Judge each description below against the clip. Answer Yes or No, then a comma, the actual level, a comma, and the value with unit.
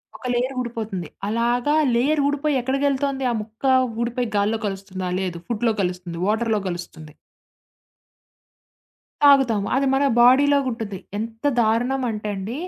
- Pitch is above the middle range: Yes, high, 235 Hz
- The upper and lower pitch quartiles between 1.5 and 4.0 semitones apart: No, average, 4.6 semitones